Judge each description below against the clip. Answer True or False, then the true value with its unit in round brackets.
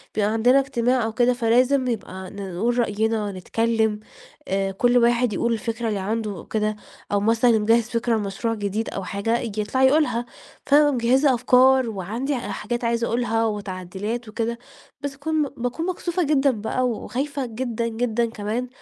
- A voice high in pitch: True (230 Hz)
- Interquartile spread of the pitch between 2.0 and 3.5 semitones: True (2.8 semitones)